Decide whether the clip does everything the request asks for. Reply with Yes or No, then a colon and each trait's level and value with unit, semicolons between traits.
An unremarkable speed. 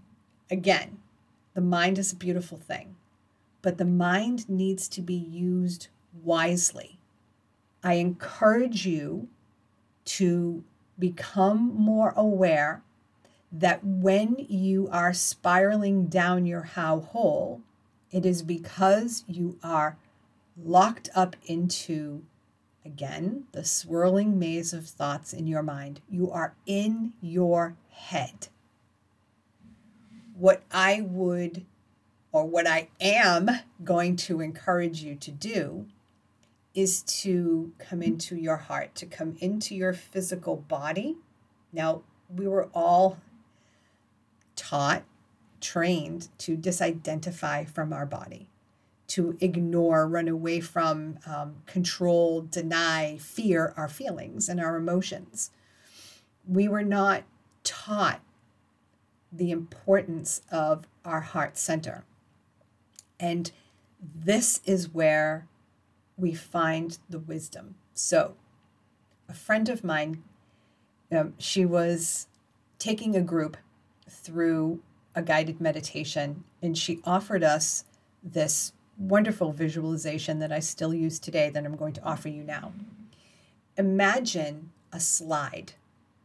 No: slow, 110 wpm